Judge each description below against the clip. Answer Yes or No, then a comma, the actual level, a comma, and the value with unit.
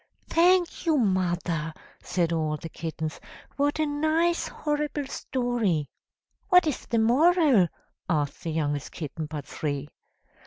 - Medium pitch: No, high, 200 Hz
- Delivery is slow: Yes, slow, 125 wpm